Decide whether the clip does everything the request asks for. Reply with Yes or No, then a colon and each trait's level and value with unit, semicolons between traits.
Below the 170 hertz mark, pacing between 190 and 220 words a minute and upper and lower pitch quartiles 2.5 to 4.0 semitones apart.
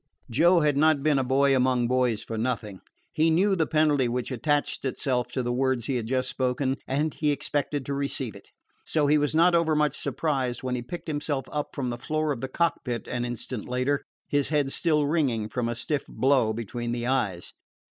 Yes: low, 135 Hz; fast, 205 wpm; average, 3.4 semitones